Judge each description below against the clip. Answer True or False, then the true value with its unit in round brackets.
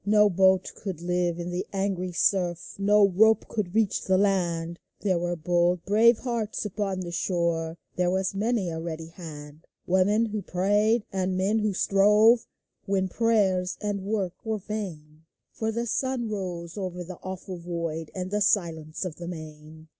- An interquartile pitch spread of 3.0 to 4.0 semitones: True (3.3 semitones)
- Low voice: False (185 Hz)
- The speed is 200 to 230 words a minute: False (170 wpm)